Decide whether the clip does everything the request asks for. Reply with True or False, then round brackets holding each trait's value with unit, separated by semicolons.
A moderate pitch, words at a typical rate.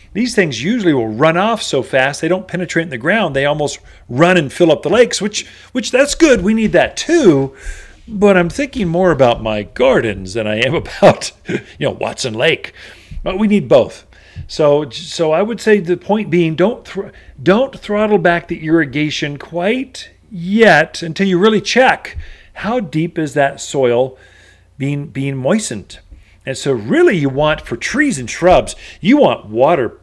True (170 Hz; 180 wpm)